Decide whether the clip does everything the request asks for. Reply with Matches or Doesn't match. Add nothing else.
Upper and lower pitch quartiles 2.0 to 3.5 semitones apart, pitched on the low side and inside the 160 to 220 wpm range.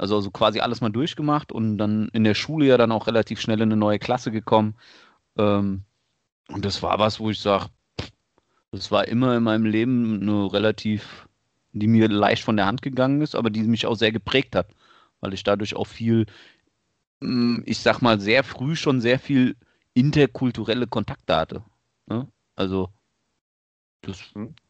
Matches